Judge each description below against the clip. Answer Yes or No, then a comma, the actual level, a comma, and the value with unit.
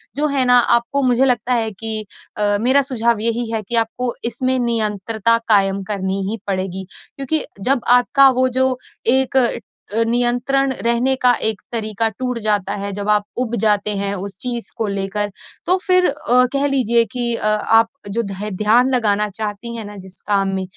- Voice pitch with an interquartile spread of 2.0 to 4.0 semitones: Yes, average, 3.4 semitones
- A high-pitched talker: Yes, high, 230 Hz